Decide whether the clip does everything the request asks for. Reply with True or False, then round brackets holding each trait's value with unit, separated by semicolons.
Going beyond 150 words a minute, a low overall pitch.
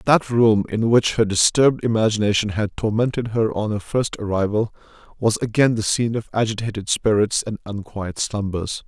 True (160 wpm; 110 Hz)